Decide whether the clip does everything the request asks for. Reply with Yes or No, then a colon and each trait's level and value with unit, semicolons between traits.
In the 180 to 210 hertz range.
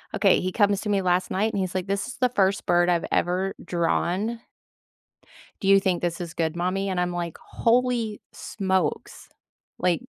Yes: high, 190 Hz